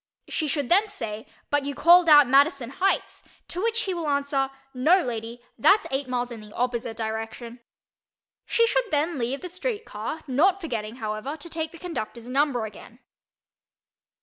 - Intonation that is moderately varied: No, wide, 6.1 semitones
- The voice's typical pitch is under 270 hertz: No, very high, 280 Hz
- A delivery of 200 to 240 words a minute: No, average, 165 wpm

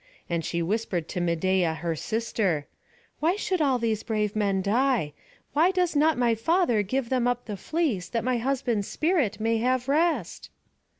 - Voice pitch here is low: No, high, 230 Hz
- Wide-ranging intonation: Yes, wide, 5.8 semitones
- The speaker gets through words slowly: No, average, 170 wpm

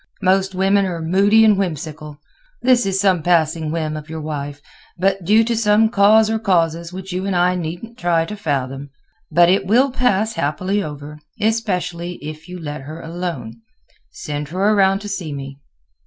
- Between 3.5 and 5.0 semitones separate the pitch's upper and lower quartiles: Yes, average, 4.5 semitones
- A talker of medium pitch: Yes, medium, 180 Hz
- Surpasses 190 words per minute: No, average, 170 wpm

